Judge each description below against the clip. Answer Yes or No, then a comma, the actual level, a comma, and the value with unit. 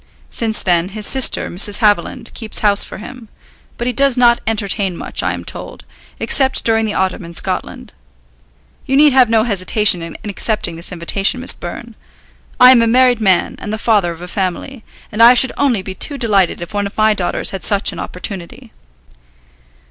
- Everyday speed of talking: Yes, average, 190 wpm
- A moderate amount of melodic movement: Yes, average, 4.1 semitones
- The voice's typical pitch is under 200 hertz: No, high, 215 Hz